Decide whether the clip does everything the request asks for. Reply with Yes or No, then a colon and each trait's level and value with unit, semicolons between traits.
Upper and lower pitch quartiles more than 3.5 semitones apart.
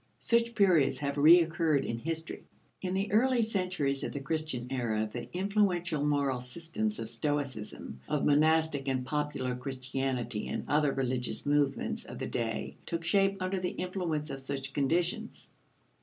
Yes: average, 5.0 semitones